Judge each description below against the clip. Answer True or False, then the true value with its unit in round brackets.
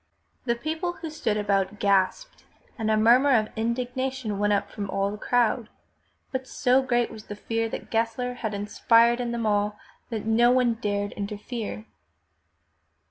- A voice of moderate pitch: False (225 Hz)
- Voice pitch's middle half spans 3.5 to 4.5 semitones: False (3.0 semitones)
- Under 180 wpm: True (170 wpm)